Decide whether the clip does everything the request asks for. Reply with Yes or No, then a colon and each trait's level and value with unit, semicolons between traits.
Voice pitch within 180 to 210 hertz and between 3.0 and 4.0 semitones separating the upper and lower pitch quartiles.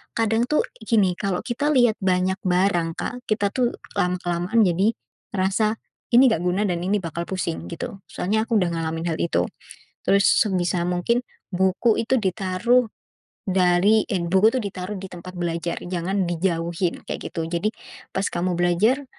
Yes: medium, 185 Hz; average, 3.4 semitones